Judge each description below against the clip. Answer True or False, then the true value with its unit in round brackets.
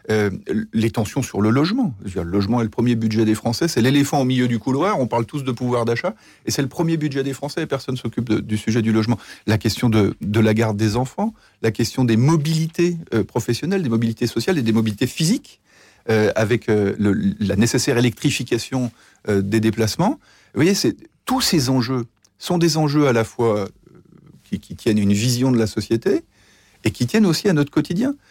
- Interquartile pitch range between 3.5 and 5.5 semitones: True (4.6 semitones)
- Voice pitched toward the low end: True (120 Hz)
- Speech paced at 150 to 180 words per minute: False (215 wpm)